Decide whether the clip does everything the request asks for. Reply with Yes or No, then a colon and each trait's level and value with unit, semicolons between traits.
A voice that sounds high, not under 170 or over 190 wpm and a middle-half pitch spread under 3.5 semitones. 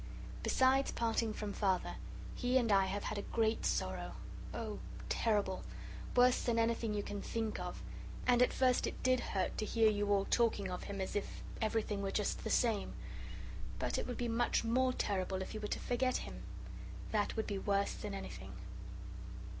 Yes: high, 220 Hz; average, 185 wpm; average, 3.0 semitones